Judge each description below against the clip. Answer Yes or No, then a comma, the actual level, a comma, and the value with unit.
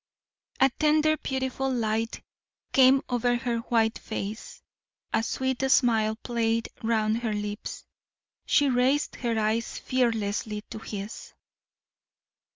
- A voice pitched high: Yes, high, 230 Hz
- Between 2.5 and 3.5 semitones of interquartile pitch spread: Yes, average, 2.9 semitones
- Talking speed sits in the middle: No, slow, 110 wpm